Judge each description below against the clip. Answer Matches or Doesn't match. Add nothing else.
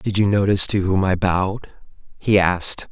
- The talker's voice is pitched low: Matches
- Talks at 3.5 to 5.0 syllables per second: Doesn't match